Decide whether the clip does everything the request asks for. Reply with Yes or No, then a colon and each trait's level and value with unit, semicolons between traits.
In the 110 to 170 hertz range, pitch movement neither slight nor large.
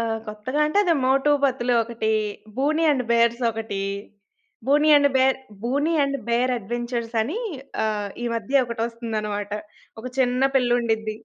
No: high, 240 Hz; average, 3.0 semitones